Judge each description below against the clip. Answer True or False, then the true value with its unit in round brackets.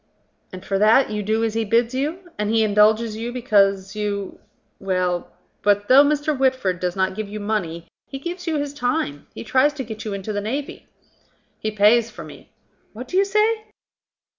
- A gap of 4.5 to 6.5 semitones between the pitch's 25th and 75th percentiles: True (5.0 semitones)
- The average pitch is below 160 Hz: False (220 Hz)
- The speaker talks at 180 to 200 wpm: True (190 wpm)